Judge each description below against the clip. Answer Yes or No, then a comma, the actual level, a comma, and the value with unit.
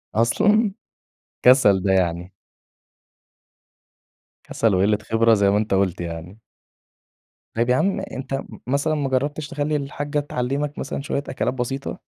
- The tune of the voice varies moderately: No, wide, 6.1 semitones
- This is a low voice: Yes, low, 125 Hz